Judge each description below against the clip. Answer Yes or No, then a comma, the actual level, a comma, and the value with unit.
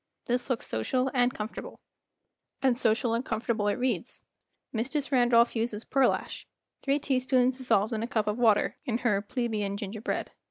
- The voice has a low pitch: No, high, 240 Hz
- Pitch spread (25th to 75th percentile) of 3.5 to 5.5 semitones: No, average, 2.8 semitones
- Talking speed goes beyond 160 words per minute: No, average, 155 wpm